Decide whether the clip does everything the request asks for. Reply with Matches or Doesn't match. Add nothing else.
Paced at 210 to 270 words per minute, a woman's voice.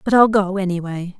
Doesn't match